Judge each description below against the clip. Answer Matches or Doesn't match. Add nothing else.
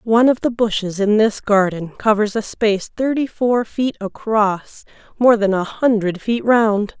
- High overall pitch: Matches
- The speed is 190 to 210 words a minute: Doesn't match